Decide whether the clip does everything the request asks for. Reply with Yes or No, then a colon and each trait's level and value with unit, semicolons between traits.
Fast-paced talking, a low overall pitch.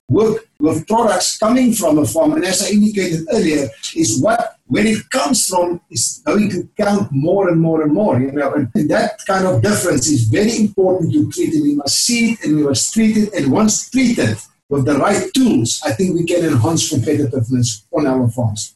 No: fast, 210 wpm; medium, 185 Hz